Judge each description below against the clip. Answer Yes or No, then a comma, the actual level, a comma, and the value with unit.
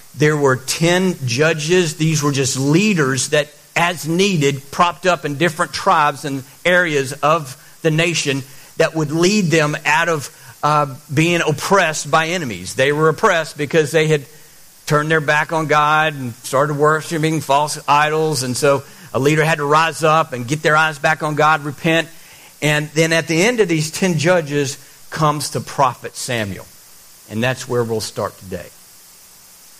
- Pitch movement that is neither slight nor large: No, narrow, 2.2 semitones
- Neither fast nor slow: Yes, average, 165 wpm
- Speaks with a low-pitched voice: No, medium, 155 Hz